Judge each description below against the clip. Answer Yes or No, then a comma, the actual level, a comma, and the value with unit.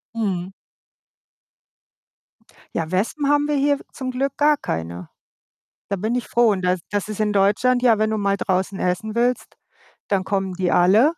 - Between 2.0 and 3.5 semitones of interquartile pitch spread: No, average, 5.0 semitones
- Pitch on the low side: No, high, 210 Hz